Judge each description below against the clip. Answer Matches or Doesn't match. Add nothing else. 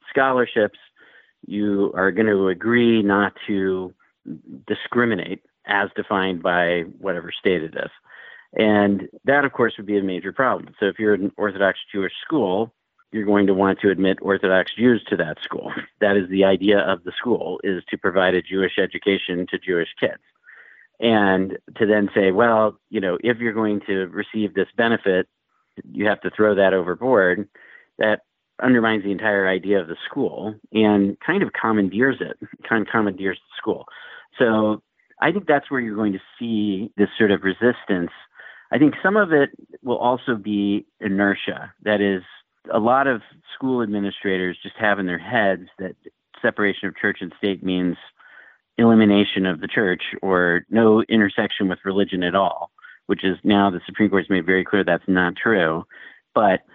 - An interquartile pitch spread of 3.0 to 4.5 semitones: Doesn't match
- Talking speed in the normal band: Matches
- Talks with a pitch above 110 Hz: Doesn't match